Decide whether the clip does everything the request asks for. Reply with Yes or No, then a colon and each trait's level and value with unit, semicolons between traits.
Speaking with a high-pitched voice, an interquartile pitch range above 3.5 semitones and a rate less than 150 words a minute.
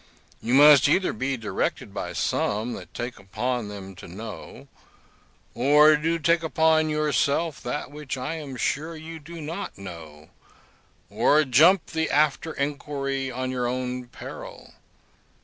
No: medium, 140 Hz; average, 4.1 semitones; average, 140 wpm